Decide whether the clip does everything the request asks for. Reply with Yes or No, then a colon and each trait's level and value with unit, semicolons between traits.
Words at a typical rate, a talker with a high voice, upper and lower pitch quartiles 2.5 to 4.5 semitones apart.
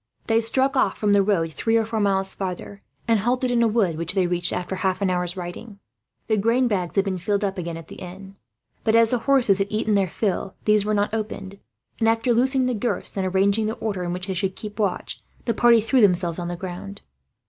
No: fast, 235 wpm; high, 200 Hz; average, 3.4 semitones